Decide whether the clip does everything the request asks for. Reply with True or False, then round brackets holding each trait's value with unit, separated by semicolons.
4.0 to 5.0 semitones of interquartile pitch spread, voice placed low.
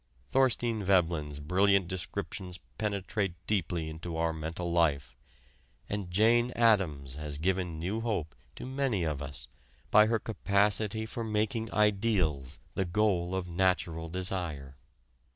True (4.6 semitones; 95 Hz)